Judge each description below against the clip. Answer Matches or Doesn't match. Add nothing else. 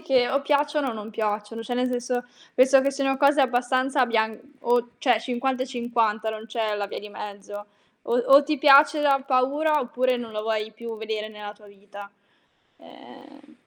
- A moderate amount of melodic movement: Matches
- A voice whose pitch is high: Matches